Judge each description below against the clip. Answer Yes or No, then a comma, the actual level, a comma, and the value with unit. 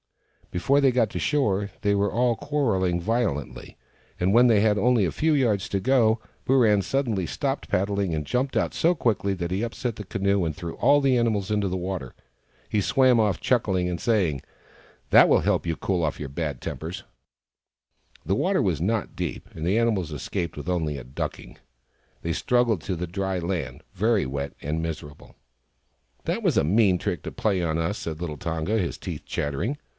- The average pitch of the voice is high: No, very low, 95 Hz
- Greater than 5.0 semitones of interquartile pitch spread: Yes, wide, 5.4 semitones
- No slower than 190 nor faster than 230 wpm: Yes, average, 195 wpm